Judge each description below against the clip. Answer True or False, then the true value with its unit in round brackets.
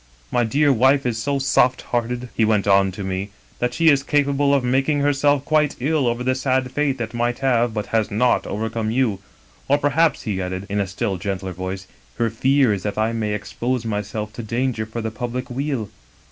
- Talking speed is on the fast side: True (215 wpm)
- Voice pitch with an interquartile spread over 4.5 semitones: False (4.2 semitones)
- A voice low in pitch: True (120 Hz)